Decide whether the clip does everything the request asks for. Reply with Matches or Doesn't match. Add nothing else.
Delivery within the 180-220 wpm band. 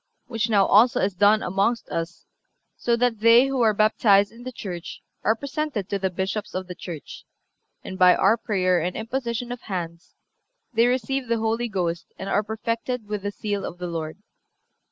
Matches